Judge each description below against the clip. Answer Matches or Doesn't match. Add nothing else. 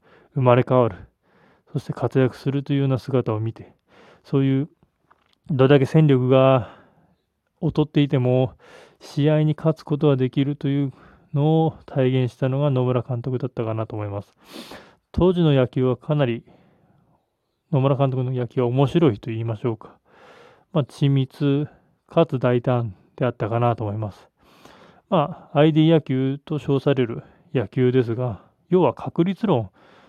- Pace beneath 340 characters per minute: Matches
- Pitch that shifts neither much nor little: Matches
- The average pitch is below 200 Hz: Matches